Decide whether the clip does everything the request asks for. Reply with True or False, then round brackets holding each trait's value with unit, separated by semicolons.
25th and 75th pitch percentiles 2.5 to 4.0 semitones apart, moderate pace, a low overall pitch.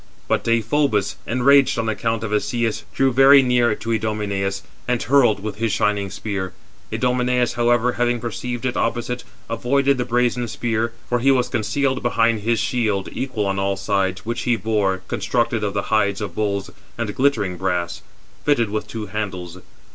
True (3.1 semitones; 165 wpm; 115 Hz)